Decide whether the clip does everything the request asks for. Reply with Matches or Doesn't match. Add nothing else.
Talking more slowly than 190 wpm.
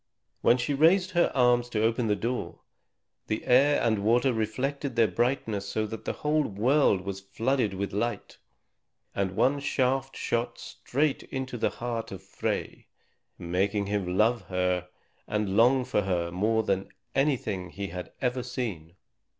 Matches